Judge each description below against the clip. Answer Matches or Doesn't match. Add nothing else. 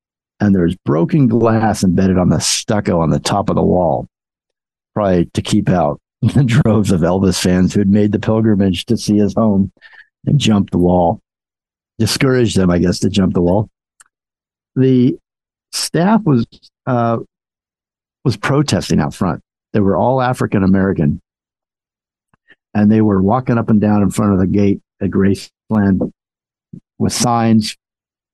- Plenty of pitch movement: Doesn't match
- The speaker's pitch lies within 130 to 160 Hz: Doesn't match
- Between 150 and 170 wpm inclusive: Matches